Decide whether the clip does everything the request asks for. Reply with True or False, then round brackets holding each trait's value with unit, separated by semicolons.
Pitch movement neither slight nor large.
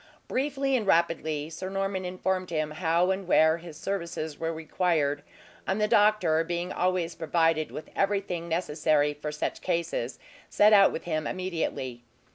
True (3.2 semitones)